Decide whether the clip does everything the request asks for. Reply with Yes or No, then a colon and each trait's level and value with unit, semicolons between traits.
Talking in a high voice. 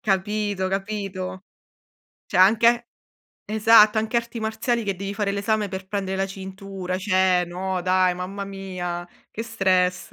Yes: high, 195 Hz